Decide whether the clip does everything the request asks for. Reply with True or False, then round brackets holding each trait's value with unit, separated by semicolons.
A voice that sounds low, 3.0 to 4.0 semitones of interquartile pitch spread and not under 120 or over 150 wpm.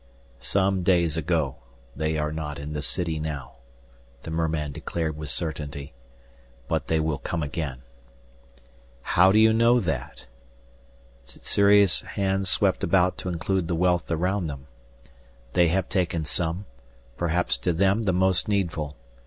True (85 Hz; 3.6 semitones; 140 wpm)